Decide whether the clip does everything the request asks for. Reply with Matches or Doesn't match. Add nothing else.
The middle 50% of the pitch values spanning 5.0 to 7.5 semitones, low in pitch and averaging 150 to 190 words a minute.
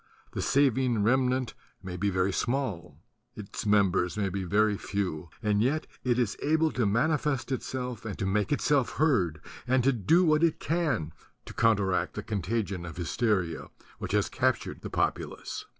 Matches